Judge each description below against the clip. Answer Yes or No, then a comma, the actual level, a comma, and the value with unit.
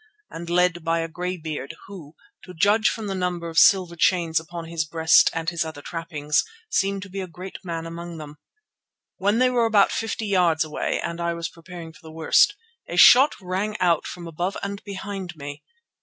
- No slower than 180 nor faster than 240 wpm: Yes, average, 200 wpm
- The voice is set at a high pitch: No, medium, 175 Hz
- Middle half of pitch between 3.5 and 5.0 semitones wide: No, average, 3.0 semitones